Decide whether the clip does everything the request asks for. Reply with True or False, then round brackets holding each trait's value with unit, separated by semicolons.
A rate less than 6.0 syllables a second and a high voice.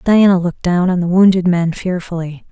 False (5.5 syllables/s; 180 Hz)